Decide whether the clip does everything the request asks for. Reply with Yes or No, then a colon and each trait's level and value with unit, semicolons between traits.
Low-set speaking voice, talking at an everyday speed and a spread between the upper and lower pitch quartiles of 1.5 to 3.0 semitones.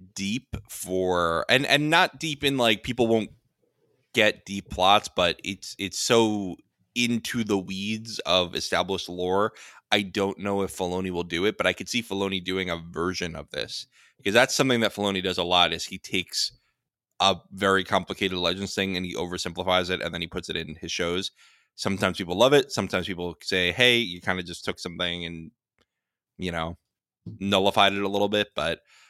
Yes: very low, 95 Hz; average, 190 wpm; narrow, 2.5 semitones